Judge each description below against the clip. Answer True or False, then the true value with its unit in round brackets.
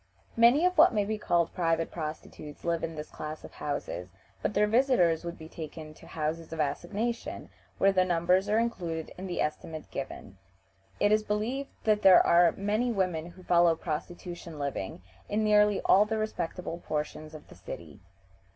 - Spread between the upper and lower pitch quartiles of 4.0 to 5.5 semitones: True (4.8 semitones)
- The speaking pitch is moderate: True (175 Hz)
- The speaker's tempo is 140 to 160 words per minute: False (175 wpm)